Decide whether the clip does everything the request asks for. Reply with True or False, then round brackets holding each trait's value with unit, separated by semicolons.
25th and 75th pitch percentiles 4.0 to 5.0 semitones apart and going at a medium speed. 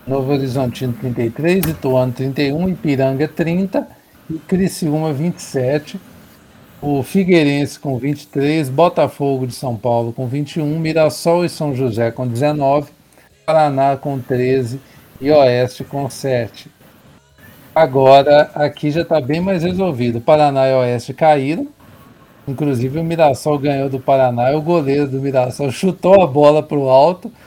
False (3.2 semitones; 135 wpm)